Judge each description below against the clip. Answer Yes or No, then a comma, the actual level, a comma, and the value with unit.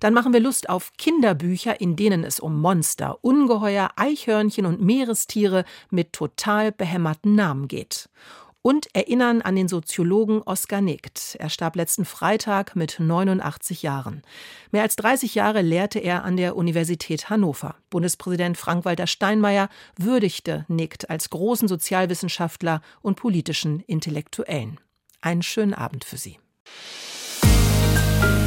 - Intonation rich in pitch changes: No, average, 4.5 semitones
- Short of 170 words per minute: Yes, slow, 125 wpm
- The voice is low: No, medium, 180 Hz